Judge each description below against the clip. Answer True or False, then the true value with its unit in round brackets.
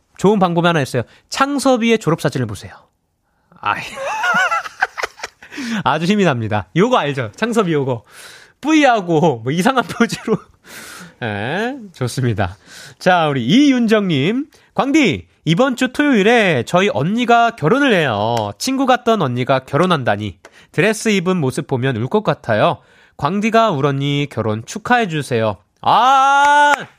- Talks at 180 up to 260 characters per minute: False (275 characters per minute)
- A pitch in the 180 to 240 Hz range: True (185 Hz)